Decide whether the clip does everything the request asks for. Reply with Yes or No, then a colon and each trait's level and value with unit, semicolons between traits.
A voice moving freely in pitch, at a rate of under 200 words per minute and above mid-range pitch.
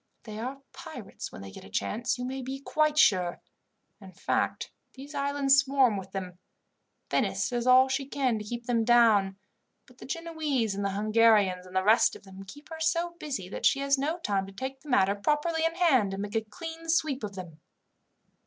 No: wide, 5.9 semitones; fast, 205 wpm; high, 245 Hz